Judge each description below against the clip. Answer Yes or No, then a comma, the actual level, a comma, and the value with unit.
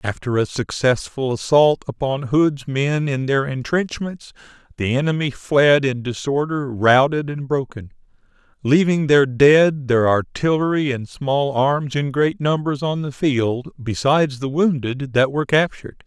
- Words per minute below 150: Yes, average, 140 wpm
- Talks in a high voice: No, medium, 140 Hz